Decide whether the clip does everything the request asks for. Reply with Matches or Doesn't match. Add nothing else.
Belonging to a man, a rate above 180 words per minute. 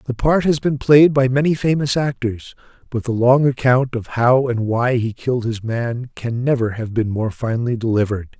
Matches